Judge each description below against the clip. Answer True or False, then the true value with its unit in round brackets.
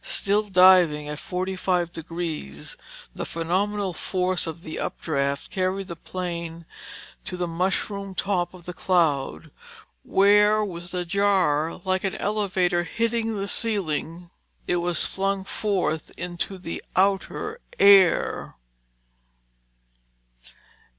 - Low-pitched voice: False (180 Hz)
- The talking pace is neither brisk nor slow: False (110 wpm)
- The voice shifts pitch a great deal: False (2.7 semitones)